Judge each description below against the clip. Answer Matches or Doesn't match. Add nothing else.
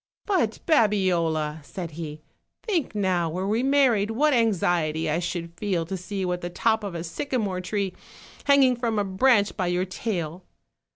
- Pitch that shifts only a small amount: Doesn't match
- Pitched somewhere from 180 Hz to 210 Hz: Matches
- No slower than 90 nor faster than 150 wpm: Doesn't match